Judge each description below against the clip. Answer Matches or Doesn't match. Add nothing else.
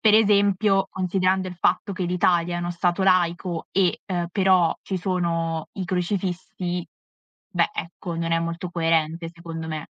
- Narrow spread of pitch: Matches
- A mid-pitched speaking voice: Matches